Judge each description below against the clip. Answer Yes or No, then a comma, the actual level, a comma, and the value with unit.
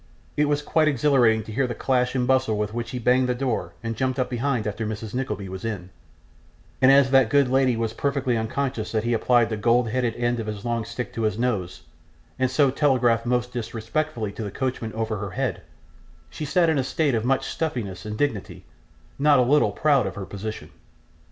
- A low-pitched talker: Yes, low, 120 Hz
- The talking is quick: Yes, fast, 215 wpm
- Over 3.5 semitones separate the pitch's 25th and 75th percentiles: No, average, 3.2 semitones